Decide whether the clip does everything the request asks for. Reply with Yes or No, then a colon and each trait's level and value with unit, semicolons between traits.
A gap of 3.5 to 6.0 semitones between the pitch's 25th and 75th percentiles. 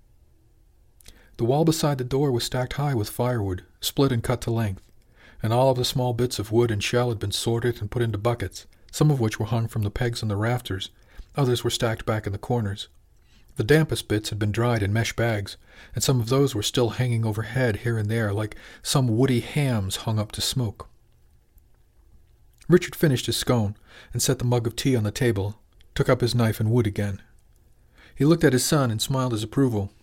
No: average, 3.0 semitones